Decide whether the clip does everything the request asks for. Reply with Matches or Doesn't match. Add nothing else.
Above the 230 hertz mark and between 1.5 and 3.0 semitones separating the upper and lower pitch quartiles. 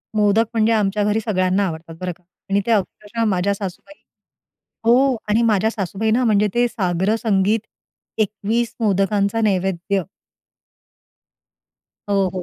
Doesn't match